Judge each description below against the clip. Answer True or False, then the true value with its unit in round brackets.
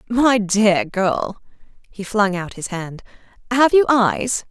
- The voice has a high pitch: True (210 Hz)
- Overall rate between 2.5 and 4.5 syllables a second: True (3.5 syllables/s)